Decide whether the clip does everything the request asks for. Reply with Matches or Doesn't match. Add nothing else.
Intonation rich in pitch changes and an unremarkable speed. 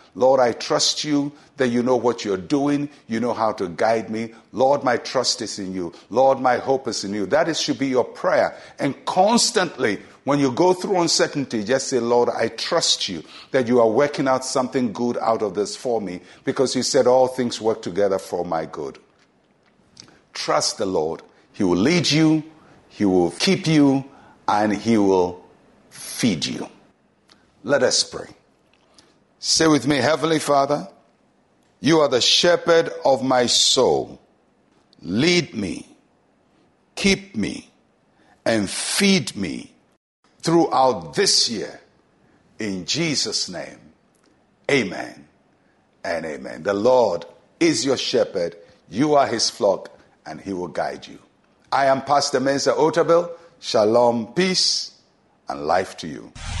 Matches